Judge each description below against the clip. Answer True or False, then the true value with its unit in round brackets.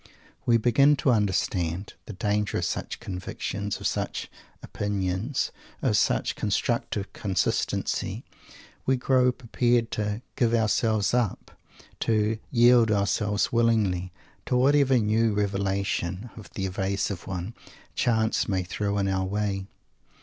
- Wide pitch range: False (3.2 semitones)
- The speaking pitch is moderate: False (105 Hz)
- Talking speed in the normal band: False (120 wpm)